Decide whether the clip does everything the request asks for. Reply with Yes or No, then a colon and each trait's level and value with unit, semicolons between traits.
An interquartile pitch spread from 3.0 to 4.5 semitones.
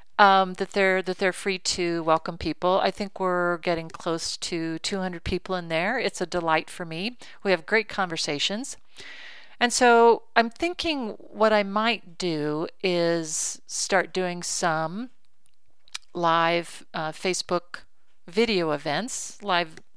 Yes: average, 3.4 semitones